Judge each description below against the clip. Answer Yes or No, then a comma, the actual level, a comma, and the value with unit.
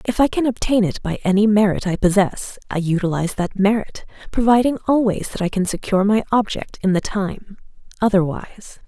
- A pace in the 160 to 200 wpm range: Yes, average, 175 wpm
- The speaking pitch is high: Yes, high, 205 Hz